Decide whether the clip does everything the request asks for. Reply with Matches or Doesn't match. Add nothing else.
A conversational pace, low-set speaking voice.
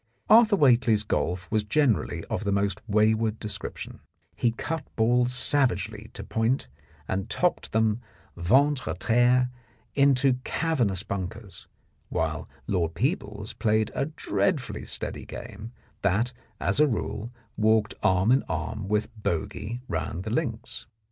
Doesn't match